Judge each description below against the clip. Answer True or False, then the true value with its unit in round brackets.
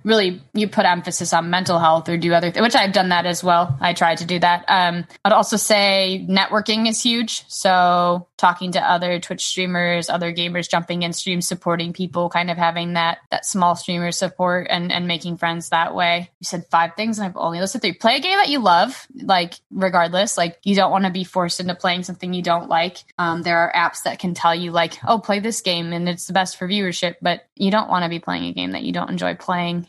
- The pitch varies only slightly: True (1.8 semitones)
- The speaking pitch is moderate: True (175 Hz)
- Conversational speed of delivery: False (240 wpm)